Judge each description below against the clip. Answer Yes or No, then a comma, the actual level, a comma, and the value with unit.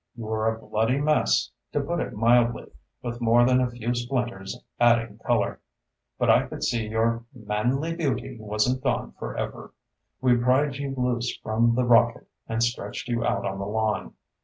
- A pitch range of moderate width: No, narrow, 2.2 semitones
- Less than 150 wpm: No, average, 170 wpm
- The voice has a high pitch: No, low, 120 Hz